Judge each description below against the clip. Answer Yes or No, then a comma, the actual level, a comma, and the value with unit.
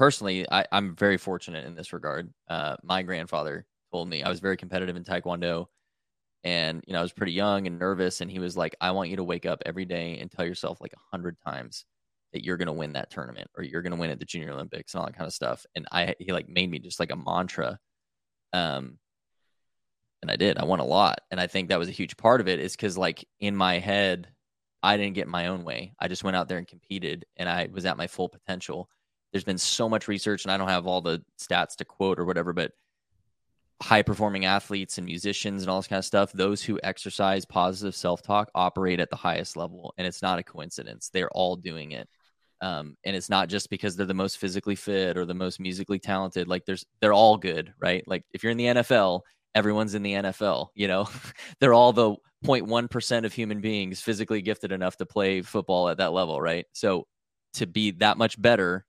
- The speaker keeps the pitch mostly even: Yes, narrow, 2.2 semitones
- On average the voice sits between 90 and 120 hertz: Yes, very low, 95 Hz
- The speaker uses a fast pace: Yes, fast, 230 wpm